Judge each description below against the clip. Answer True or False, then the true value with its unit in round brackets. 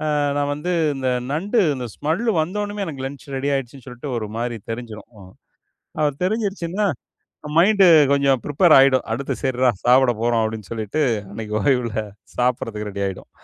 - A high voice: False (135 Hz)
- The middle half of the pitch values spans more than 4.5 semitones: True (5.0 semitones)